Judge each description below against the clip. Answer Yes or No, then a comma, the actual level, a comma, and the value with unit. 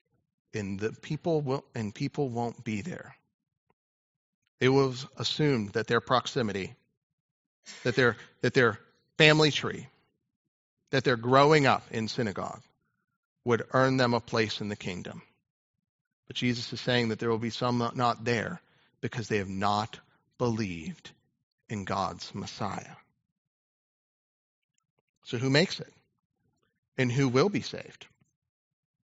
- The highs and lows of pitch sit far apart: No, average, 3.6 semitones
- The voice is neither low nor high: No, low, 125 Hz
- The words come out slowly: Yes, slow, 130 wpm